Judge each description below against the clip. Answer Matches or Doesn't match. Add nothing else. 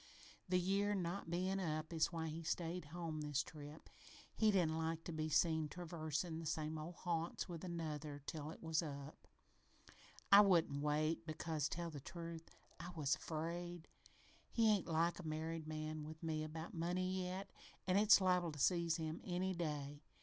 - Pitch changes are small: Matches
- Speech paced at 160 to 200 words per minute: Matches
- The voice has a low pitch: Doesn't match